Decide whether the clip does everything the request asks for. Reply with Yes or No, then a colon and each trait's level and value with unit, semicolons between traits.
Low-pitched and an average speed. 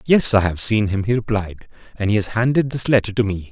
No: low, 110 Hz; fast, 255 wpm